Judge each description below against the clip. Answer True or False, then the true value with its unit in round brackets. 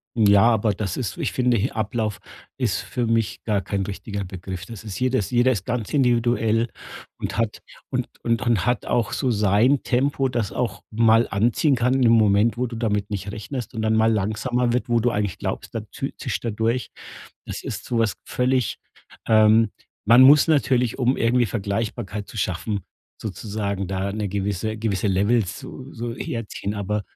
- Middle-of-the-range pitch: False (110 Hz)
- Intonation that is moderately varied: True (3.0 semitones)